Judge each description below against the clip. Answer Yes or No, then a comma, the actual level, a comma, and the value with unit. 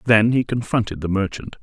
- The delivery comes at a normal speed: Yes, average, 185 wpm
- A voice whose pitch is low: Yes, low, 110 Hz